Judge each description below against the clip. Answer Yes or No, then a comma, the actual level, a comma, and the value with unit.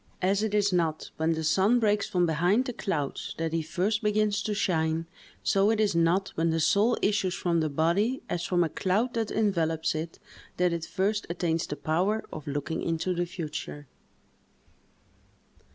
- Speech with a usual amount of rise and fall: Yes, average, 4.2 semitones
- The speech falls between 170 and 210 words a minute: Yes, average, 180 wpm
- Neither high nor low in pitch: Yes, medium, 180 Hz